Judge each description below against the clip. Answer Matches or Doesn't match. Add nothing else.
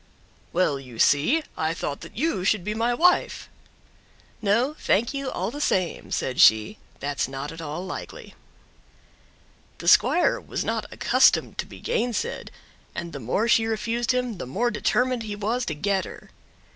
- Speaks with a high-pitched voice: Matches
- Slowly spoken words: Doesn't match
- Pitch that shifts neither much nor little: Doesn't match